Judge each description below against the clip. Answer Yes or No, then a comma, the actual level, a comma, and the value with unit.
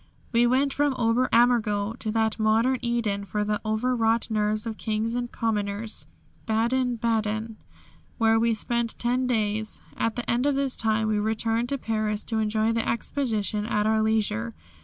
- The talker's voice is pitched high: Yes, high, 225 Hz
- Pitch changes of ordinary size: No, narrow, 1.8 semitones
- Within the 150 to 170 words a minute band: Yes, average, 165 wpm